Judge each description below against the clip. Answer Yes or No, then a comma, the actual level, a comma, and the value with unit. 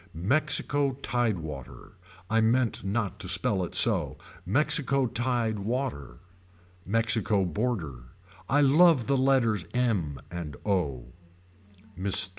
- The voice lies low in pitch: Yes, low, 110 Hz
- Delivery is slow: Yes, slow, 110 wpm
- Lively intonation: Yes, wide, 6.1 semitones